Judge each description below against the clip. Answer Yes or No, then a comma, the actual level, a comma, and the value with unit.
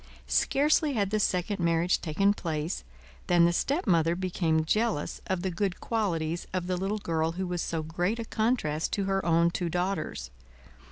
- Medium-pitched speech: Yes, medium, 180 Hz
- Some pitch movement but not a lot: Yes, average, 3.3 semitones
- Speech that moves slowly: No, average, 170 wpm